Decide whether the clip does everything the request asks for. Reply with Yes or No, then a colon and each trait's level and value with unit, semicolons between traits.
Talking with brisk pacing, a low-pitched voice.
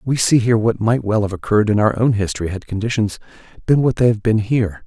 Yes: fast, 245 wpm; low, 110 Hz